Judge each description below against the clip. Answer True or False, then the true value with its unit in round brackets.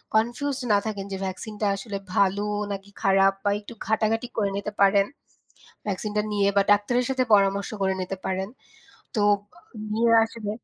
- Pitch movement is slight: True (2.1 semitones)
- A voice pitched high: True (205 Hz)